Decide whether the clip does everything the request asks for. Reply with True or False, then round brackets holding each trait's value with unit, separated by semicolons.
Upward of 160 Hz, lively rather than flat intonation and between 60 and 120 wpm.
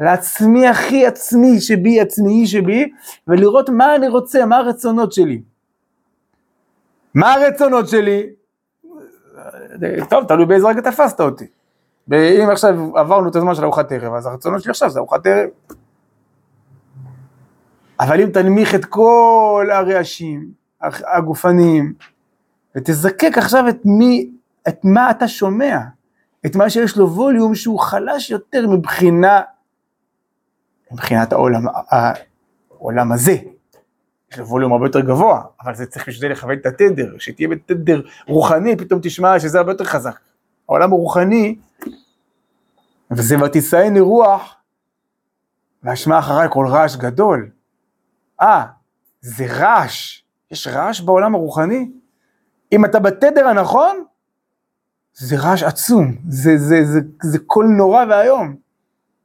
True (190 Hz; 7.2 semitones; 115 wpm)